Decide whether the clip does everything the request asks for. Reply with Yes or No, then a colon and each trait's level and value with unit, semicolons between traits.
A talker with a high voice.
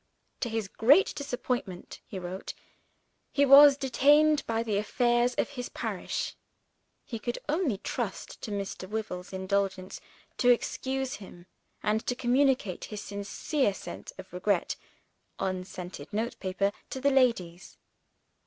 Yes: high, 230 Hz